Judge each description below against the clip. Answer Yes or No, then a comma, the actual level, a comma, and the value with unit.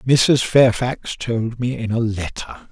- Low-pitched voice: Yes, low, 120 Hz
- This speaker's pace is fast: No, average, 155 wpm